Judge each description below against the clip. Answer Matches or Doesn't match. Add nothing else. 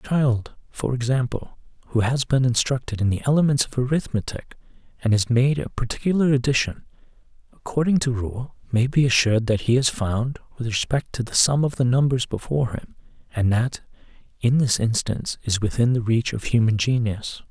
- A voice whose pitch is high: Doesn't match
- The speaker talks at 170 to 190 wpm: Matches